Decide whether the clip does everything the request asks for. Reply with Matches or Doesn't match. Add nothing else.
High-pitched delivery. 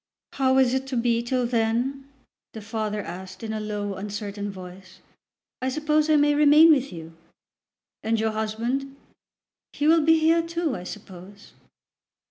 Matches